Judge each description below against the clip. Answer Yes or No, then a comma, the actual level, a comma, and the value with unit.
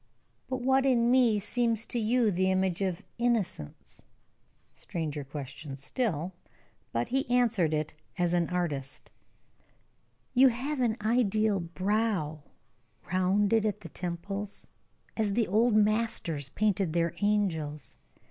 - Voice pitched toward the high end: Yes, high, 200 Hz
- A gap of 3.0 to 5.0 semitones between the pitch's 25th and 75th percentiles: No, wide, 5.4 semitones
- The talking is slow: Yes, slow, 120 wpm